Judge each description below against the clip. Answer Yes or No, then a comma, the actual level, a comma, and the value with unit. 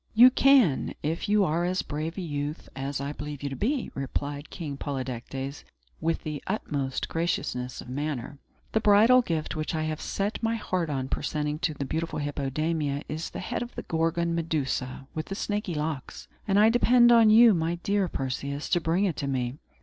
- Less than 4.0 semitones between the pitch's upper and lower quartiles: No, wide, 5.4 semitones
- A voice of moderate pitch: Yes, medium, 155 Hz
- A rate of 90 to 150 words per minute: No, average, 190 wpm